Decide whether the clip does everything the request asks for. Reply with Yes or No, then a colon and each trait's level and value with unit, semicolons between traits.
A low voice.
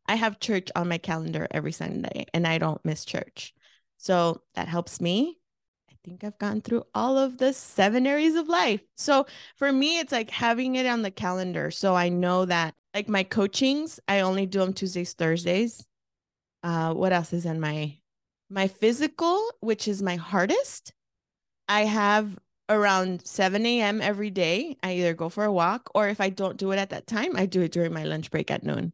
No: high, 195 Hz